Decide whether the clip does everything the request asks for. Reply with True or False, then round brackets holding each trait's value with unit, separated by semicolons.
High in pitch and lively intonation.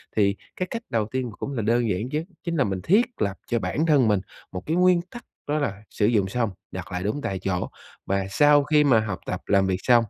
False (115 Hz; 7.0 semitones)